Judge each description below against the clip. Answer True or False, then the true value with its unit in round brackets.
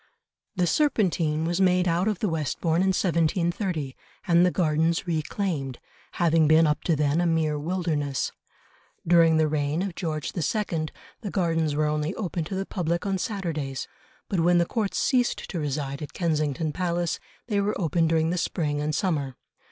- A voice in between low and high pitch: True (165 Hz)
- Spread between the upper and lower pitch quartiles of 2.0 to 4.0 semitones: True (2.9 semitones)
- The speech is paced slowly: False (170 wpm)